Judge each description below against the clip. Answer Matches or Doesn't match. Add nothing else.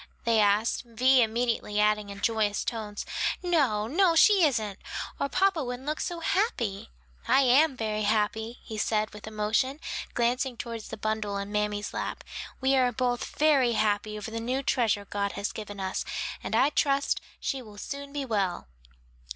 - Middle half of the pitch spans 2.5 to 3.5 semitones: Doesn't match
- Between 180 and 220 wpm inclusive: Doesn't match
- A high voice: Matches